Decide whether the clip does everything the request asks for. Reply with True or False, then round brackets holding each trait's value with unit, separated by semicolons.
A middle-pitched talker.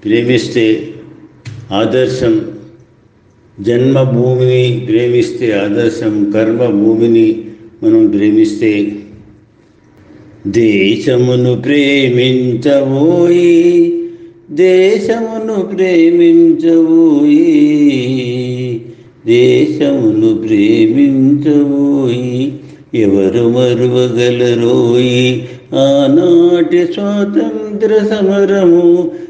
True (145 Hz)